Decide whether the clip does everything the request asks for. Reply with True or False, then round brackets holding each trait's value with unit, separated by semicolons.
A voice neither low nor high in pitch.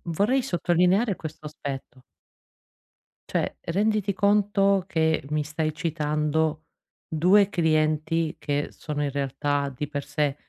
True (160 Hz)